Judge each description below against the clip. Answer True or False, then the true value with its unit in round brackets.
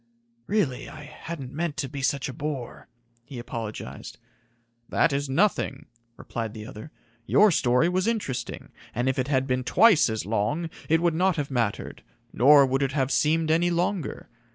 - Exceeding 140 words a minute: True (170 wpm)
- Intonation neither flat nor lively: True (4.5 semitones)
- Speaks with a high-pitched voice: False (140 Hz)